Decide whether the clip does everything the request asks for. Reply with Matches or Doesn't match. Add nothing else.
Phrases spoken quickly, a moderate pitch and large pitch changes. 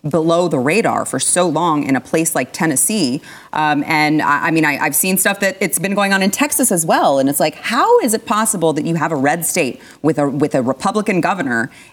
Doesn't match